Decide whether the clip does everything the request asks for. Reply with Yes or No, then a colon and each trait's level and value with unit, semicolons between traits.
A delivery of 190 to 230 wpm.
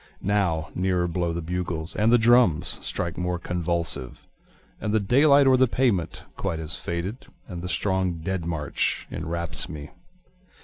No: average, 150 wpm